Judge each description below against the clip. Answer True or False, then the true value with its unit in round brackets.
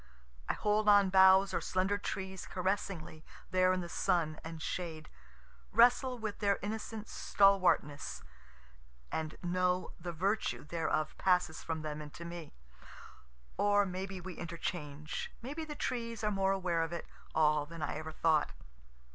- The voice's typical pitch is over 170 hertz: True (185 Hz)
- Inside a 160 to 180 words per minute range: False (150 wpm)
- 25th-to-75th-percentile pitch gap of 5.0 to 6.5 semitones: False (3.8 semitones)